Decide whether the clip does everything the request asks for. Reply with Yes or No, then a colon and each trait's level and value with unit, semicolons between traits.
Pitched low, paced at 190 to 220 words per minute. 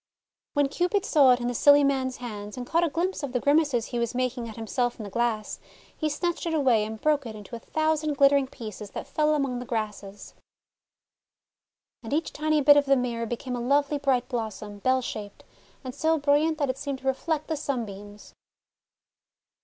No: very high, 260 Hz; average, 200 wpm